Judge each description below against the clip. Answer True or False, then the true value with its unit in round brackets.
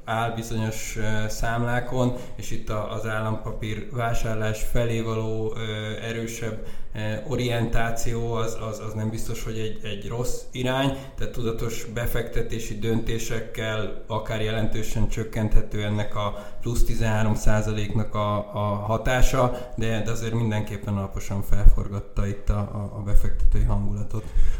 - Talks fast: False (110 wpm)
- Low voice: True (110 Hz)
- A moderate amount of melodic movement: False (1.3 semitones)